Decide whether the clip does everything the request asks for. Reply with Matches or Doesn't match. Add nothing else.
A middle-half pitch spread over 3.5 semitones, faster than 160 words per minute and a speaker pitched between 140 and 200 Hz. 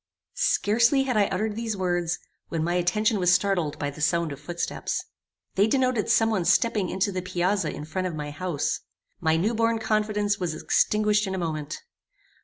Matches